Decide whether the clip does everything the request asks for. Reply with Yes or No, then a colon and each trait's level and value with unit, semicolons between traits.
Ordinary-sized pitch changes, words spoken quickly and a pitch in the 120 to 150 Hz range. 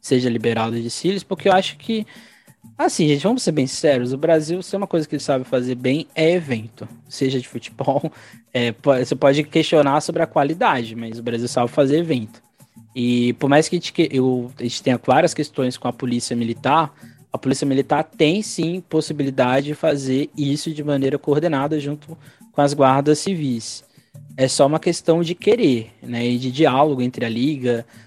Yes: average, 4.3 semitones; fast, 190 wpm; medium, 140 Hz